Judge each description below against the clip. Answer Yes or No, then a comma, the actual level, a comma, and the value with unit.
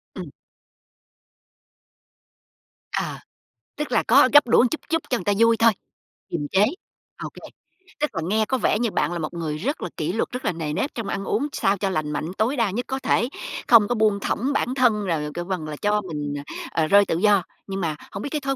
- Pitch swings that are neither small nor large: No, wide, 6.0 semitones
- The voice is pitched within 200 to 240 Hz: Yes, high, 205 Hz